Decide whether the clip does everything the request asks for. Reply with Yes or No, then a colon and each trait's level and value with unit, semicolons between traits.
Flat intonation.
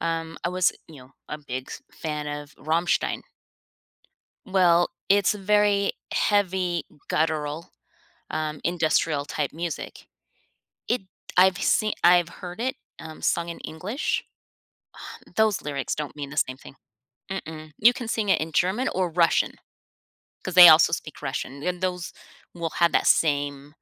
No: average, 3.6 semitones